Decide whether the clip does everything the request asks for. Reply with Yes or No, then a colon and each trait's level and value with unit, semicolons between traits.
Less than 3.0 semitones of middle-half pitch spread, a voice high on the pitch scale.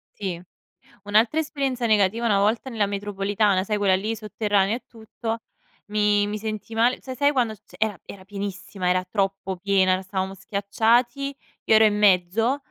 Yes: narrow, 2.6 semitones; high, 210 Hz